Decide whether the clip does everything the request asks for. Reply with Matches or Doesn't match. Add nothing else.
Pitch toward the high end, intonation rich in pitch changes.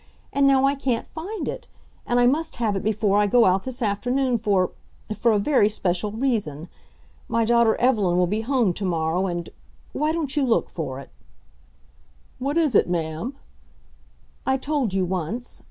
Matches